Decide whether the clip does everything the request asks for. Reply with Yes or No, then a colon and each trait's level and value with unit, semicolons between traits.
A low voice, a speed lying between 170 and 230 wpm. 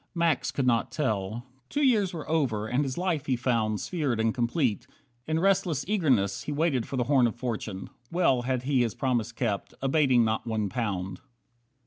Yes: low, 125 Hz; average, 180 wpm